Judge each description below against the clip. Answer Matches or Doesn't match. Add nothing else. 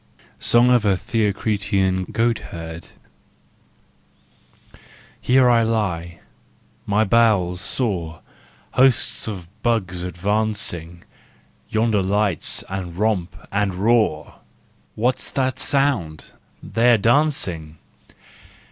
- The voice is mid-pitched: Doesn't match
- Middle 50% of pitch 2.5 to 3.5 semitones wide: Doesn't match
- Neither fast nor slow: Doesn't match